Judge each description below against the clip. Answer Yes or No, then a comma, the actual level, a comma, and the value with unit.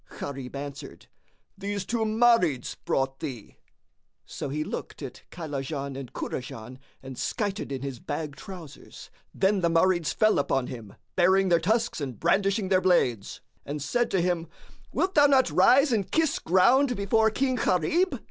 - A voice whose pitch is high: No, medium, 180 Hz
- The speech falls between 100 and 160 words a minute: Yes, average, 155 wpm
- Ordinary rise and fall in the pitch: No, wide, 7.7 semitones